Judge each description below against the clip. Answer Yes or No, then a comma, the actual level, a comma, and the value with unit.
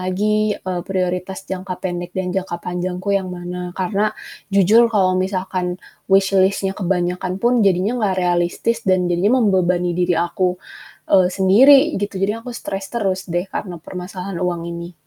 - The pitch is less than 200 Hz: Yes, medium, 185 Hz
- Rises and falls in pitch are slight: Yes, narrow, 1.5 semitones